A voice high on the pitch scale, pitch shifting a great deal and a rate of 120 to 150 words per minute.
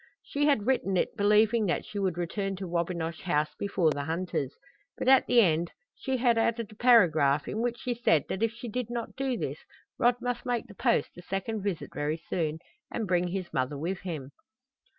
No: high, 195 Hz; wide, 5.7 semitones; fast, 205 wpm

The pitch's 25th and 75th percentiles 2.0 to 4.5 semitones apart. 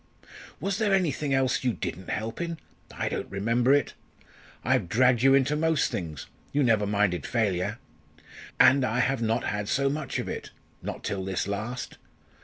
No: average, 5.1 semitones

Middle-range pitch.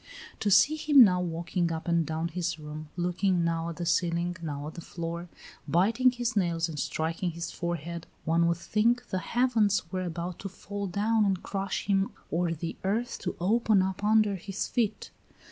Yes: medium, 180 Hz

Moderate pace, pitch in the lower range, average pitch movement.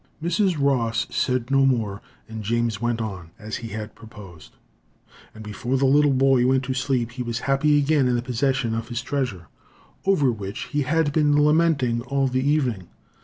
Yes: average, 180 wpm; low, 125 Hz; average, 3.5 semitones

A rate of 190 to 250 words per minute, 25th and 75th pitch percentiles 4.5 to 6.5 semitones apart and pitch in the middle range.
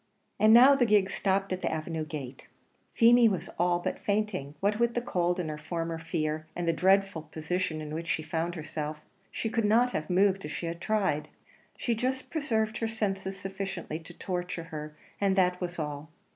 Yes: average, 195 wpm; average, 4.8 semitones; medium, 180 Hz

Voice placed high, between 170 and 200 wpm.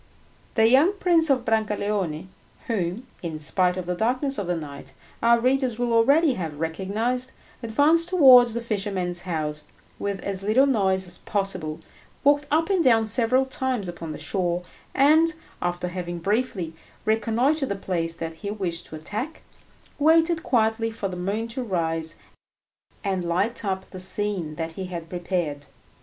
No: high, 205 Hz; average, 155 wpm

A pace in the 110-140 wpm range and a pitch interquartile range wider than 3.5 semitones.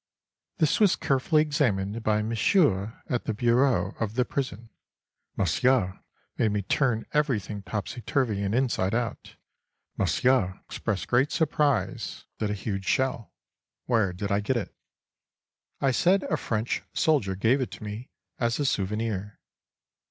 Yes: slow, 135 wpm; average, 4.4 semitones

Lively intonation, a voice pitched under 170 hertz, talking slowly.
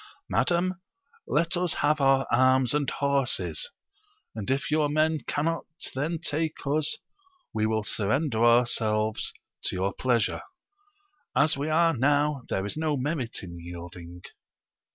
Yes: wide, 5.8 semitones; medium, 140 Hz; slow, 130 wpm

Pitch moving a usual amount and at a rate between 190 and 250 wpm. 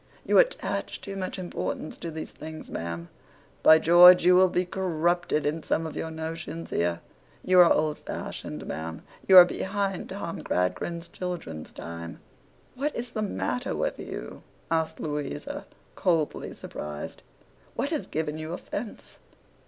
No: average, 3.3 semitones; average, 145 wpm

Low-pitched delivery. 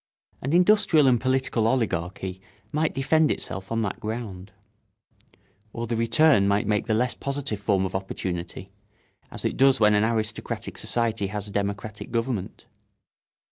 Yes: low, 110 Hz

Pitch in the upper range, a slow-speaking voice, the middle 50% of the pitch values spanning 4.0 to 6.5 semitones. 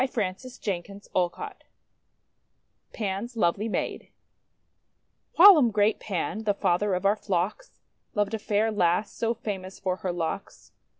No: high, 205 Hz; slow, 130 wpm; average, 3.1 semitones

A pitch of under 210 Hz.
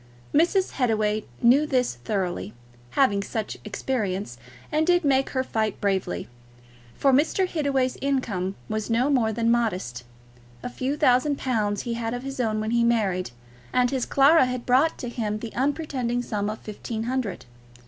No: high, 240 Hz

